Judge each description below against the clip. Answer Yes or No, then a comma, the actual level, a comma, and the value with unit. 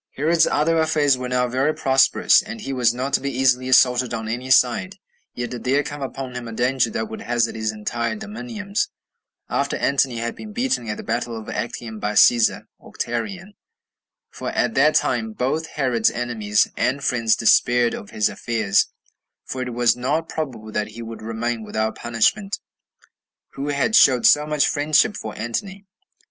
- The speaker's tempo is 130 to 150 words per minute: No, average, 180 wpm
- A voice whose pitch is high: No, low, 125 Hz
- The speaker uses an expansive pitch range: No, average, 4.3 semitones